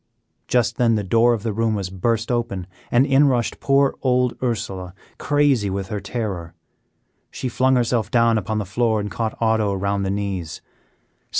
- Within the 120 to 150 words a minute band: No, average, 175 wpm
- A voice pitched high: No, low, 110 Hz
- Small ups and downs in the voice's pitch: No, average, 3.5 semitones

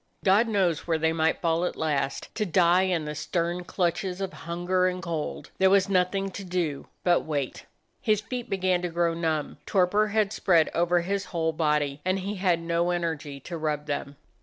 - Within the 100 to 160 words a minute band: No, average, 190 wpm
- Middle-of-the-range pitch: Yes, medium, 175 Hz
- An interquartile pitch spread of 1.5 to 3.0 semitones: Yes, average, 2.7 semitones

